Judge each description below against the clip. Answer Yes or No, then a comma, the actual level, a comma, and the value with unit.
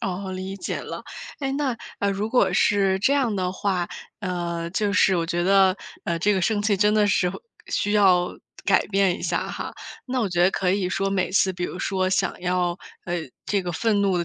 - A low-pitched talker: No, high, 190 Hz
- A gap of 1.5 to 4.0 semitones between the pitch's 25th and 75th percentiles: Yes, narrow, 2.4 semitones